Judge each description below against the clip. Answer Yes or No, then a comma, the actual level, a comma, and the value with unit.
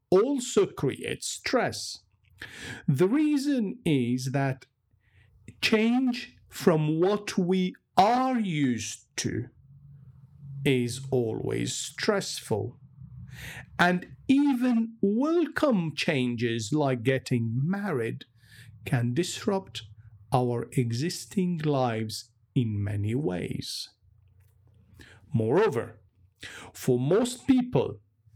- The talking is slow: Yes, slow, 75 wpm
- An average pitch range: No, wide, 8.7 semitones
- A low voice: Yes, low, 130 Hz